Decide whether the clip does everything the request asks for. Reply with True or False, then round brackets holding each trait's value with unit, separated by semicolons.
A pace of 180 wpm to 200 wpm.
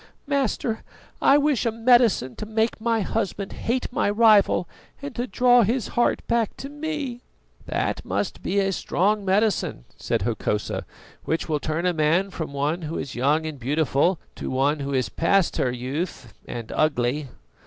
False (165 wpm)